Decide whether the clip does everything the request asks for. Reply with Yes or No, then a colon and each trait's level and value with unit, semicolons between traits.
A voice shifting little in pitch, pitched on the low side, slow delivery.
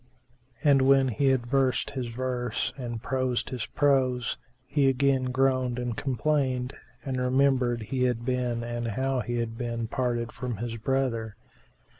No: narrow, 1.9 semitones; low, 125 Hz; average, 155 wpm